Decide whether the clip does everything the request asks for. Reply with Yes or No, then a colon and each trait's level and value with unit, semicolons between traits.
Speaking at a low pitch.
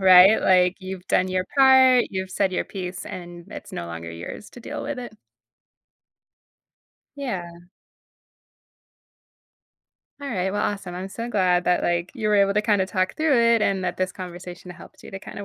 No: high, 190 Hz